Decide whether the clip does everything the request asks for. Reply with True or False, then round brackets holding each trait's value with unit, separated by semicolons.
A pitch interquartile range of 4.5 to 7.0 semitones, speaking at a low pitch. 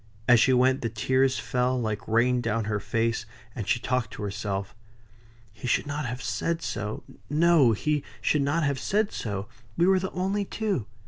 True (5.3 semitones; 125 Hz)